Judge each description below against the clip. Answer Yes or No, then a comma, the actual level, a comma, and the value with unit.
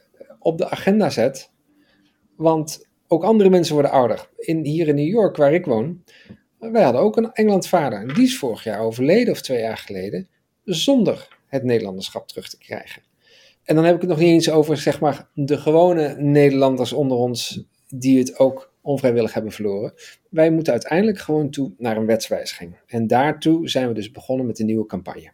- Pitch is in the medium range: Yes, medium, 150 Hz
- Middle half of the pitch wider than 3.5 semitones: Yes, average, 5.2 semitones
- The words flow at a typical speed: Yes, average, 185 wpm